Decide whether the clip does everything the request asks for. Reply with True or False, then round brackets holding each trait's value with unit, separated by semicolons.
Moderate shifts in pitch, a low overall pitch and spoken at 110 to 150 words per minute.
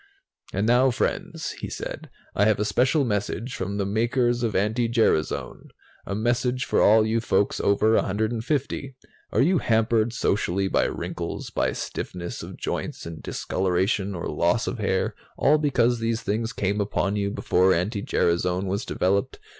False (3.4 semitones; 110 Hz; 160 wpm)